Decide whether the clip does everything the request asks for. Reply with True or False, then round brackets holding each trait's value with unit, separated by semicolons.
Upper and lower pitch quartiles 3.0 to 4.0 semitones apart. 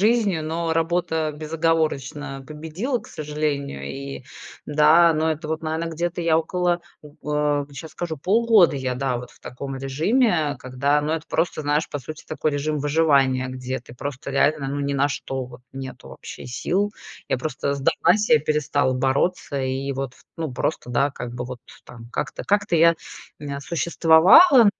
True (3.3 semitones)